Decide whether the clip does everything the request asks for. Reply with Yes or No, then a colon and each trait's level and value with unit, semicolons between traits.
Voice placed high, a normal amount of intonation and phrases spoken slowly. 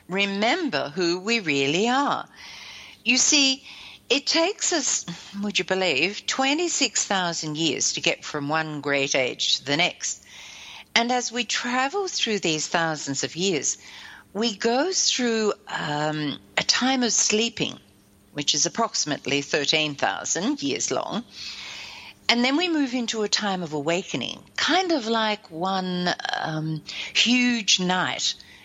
No: high, 205 Hz; wide, 7.5 semitones; slow, 130 wpm